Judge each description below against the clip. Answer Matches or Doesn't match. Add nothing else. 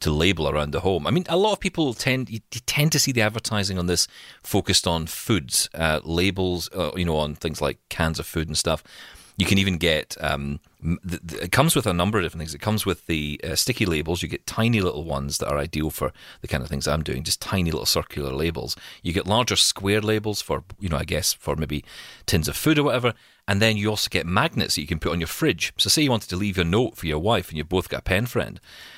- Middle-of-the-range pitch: Doesn't match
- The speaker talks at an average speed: Doesn't match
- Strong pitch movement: Matches